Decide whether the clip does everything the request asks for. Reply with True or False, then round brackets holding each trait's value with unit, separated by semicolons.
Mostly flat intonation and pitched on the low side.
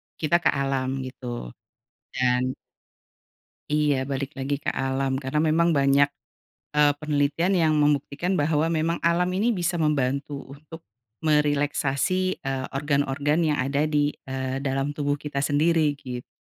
False (2.3 semitones; 145 Hz)